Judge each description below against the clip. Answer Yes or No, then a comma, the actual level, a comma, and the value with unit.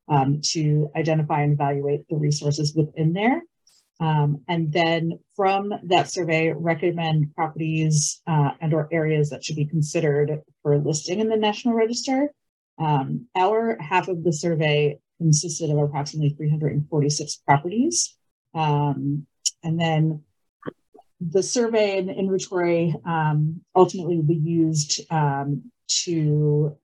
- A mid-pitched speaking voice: Yes, medium, 160 Hz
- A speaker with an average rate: No, slow, 125 wpm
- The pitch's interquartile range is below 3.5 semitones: Yes, average, 2.9 semitones